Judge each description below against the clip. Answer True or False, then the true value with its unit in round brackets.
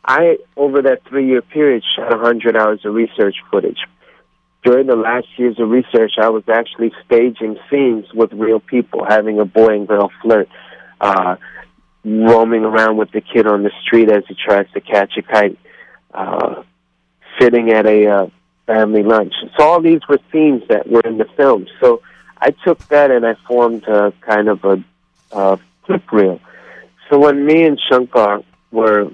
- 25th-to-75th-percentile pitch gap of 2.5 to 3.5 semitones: True (2.9 semitones)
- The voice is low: True (110 Hz)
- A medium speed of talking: True (175 wpm)